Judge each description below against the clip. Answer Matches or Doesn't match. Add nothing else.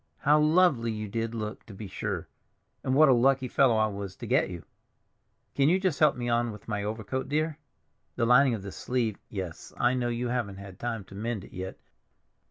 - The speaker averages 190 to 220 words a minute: Matches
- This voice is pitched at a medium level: Doesn't match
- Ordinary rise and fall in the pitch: Matches